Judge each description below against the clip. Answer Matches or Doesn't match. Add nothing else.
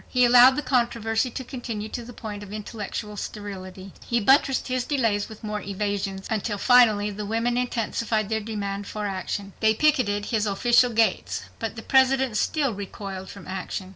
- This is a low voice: Doesn't match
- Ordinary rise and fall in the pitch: Matches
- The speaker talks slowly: Doesn't match